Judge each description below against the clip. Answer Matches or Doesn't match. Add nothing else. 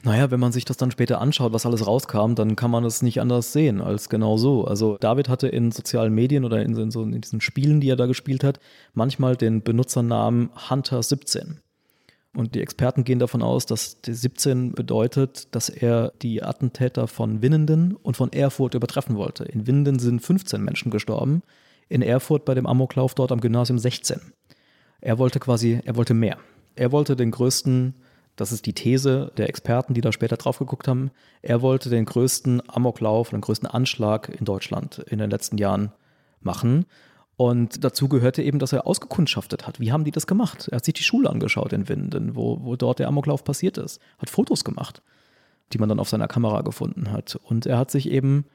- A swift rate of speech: Matches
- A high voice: Doesn't match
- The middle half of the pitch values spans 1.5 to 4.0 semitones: Matches